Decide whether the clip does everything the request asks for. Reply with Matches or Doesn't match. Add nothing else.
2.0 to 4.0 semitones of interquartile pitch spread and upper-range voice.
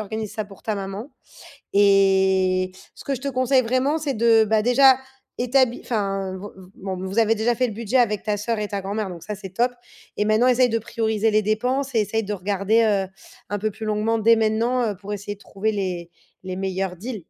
Matches